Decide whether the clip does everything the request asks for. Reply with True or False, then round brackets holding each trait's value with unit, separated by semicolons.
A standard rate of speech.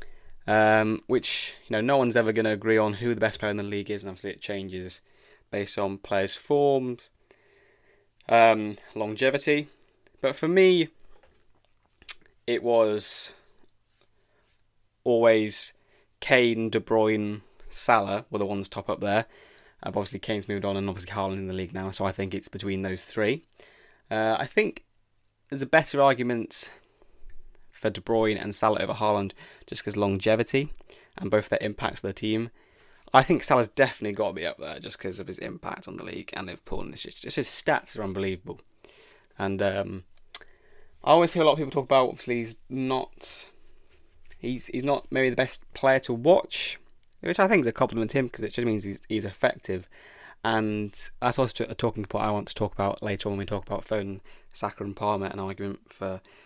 True (190 wpm)